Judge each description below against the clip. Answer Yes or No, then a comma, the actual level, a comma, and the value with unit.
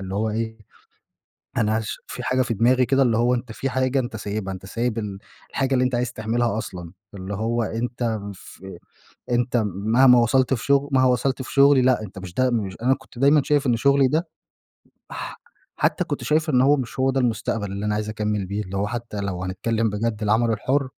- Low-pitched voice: Yes, low, 115 Hz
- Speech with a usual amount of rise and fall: Yes, average, 3.6 semitones